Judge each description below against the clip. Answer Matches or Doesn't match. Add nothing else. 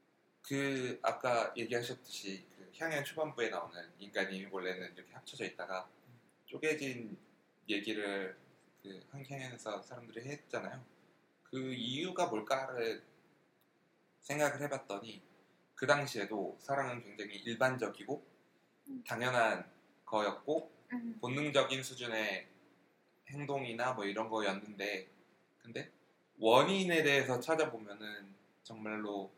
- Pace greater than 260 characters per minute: Doesn't match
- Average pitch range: Doesn't match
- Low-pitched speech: Matches